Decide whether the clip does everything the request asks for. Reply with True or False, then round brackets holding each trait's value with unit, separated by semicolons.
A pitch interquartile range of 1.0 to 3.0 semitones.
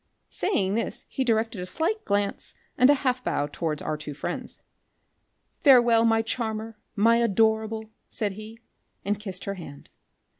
True (2.7 semitones)